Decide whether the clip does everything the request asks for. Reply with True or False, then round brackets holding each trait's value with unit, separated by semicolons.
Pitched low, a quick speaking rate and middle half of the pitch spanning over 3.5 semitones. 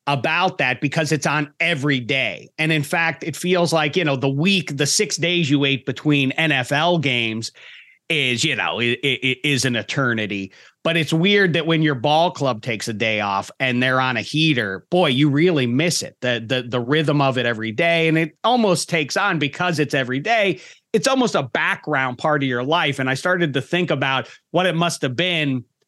False (150 Hz; 215 wpm; 4.4 semitones)